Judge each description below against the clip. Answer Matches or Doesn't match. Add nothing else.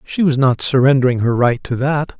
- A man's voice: Matches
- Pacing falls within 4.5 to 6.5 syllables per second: Matches